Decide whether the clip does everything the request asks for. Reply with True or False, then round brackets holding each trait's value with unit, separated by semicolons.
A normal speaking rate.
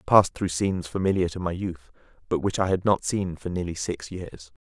False (235 wpm)